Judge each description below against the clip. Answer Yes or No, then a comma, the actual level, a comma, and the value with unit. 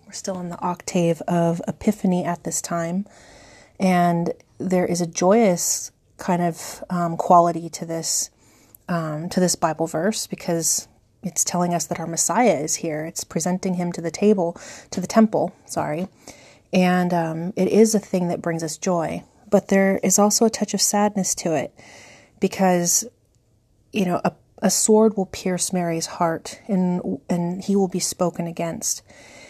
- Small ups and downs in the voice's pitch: Yes, narrow, 2.3 semitones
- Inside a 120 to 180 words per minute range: Yes, average, 165 wpm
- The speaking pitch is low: No, medium, 180 Hz